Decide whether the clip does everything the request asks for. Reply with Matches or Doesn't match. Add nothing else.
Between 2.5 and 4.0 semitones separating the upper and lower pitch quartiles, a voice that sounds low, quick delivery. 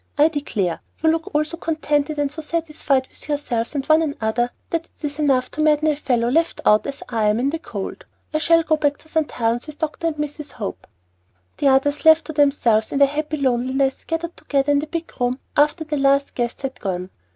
Doesn't match